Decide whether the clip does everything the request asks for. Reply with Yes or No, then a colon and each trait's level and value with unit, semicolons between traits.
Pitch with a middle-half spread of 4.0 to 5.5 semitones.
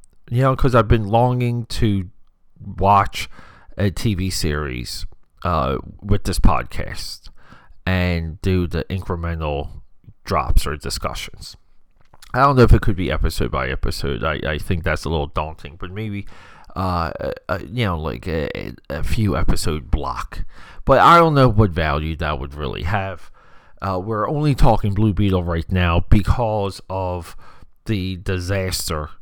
Yes: average, 4.9 semitones